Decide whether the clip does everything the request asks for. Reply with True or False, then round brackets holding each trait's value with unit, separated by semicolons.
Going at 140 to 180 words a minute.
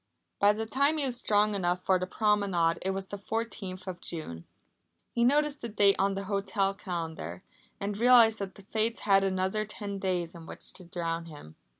False (195 wpm)